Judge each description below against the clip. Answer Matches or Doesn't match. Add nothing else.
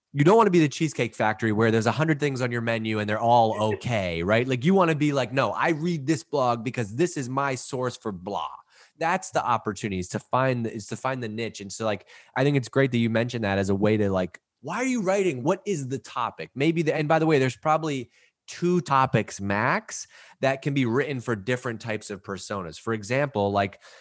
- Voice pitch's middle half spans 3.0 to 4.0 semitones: Doesn't match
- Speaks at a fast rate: Matches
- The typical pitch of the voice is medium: Doesn't match